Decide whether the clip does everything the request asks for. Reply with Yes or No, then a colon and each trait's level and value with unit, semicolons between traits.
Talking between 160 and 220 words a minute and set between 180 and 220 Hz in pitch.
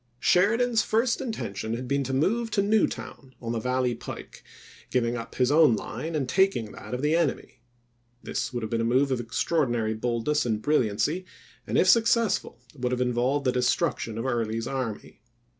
No: average, 175 wpm; low, 130 Hz